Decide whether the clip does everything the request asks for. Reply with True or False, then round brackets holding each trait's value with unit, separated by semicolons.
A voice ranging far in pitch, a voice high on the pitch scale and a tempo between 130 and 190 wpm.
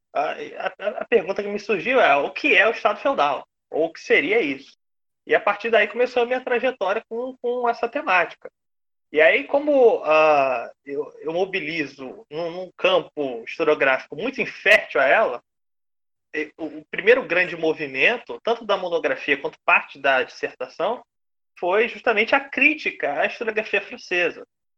True (6.8 semitones; 225 Hz; 155 wpm)